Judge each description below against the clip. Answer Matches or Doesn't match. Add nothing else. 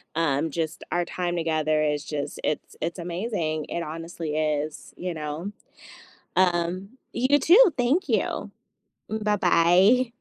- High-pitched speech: Doesn't match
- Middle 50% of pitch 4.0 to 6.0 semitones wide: Matches